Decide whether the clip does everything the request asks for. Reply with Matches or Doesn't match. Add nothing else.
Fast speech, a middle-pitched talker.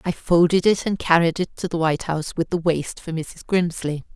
Matches